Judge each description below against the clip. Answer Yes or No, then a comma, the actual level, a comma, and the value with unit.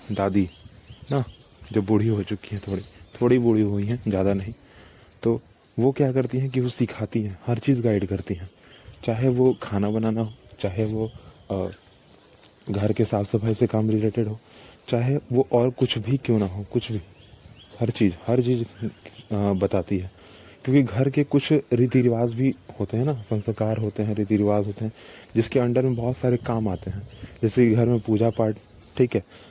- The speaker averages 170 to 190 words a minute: Yes, average, 185 wpm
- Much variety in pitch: No, average, 3.1 semitones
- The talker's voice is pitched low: Yes, low, 110 Hz